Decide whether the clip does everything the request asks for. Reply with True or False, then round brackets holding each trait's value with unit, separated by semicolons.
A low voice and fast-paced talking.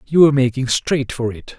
True (130 Hz; 230 wpm)